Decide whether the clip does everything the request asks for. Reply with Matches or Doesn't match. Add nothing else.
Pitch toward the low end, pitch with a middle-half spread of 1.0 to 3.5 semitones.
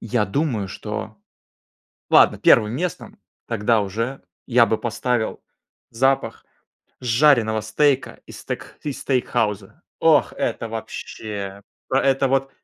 Doesn't match